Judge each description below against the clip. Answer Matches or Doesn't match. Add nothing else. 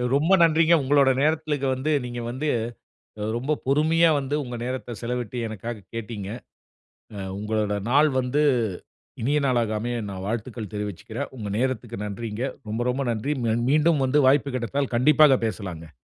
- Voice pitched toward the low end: Matches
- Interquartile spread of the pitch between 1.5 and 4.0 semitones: Doesn't match